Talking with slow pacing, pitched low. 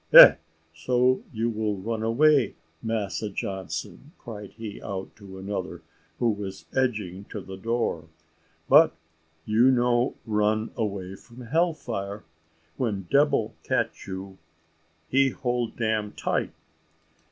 Yes: slow, 120 wpm; low, 110 Hz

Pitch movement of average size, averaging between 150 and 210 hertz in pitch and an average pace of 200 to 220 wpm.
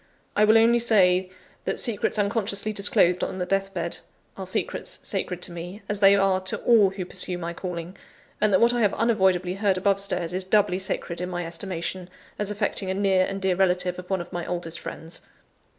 No: narrow, 2.1 semitones; high, 190 Hz; fast, 205 wpm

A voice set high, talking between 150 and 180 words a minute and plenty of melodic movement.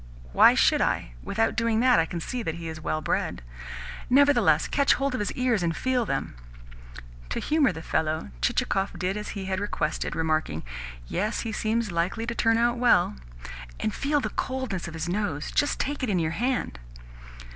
No: high, 210 Hz; average, 190 wpm; wide, 7.1 semitones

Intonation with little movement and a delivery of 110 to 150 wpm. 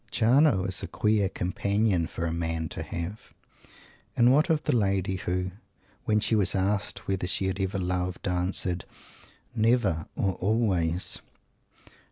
No: average, 3.2 semitones; average, 145 wpm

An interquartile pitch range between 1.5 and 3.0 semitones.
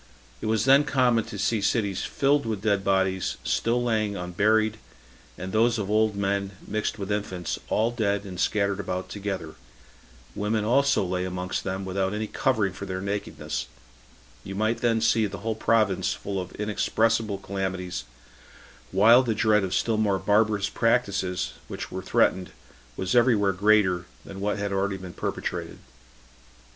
Yes: narrow, 2.5 semitones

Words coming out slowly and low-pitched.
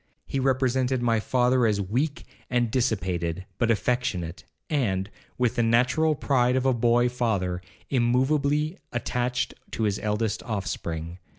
Yes: slow, 130 wpm; low, 120 Hz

